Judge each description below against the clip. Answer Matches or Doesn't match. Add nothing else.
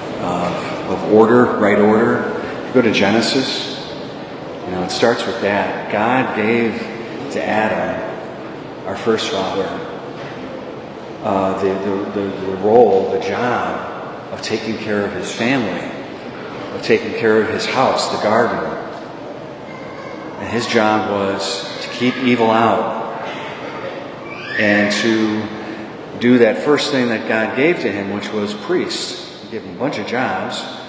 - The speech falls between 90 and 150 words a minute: Matches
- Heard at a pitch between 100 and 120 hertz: Matches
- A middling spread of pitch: Doesn't match